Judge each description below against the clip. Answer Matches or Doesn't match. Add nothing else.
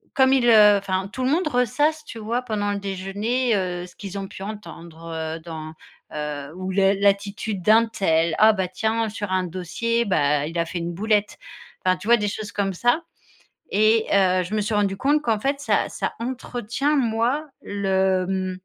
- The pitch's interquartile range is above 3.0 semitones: Matches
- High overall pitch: Matches